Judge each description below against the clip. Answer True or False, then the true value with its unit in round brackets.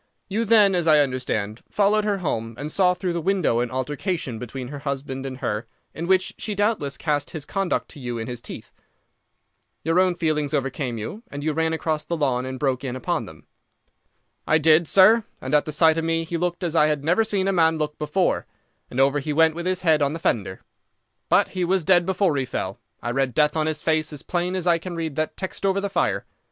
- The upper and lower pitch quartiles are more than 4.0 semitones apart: True (4.8 semitones)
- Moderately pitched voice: True (155 Hz)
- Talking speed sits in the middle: False (230 wpm)